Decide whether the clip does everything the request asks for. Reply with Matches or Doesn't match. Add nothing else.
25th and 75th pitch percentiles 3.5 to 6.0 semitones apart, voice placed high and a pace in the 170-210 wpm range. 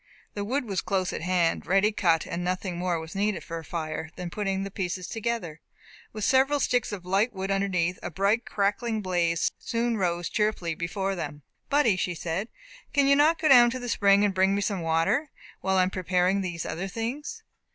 Matches